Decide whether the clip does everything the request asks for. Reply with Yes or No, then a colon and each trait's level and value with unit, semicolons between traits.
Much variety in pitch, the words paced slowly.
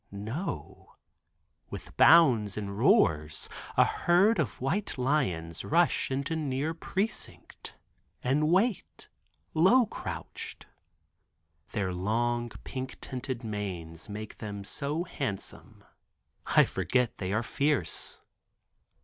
Yes: wide, 7.5 semitones; slow, 100 wpm